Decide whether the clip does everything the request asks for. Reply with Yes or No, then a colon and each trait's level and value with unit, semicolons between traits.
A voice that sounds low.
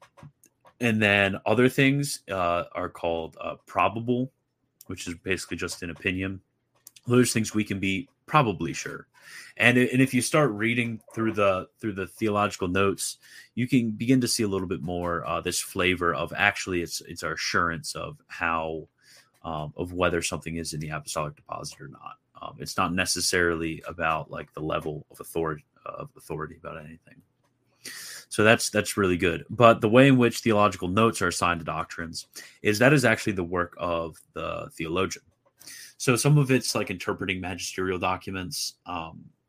Yes: very low, 95 Hz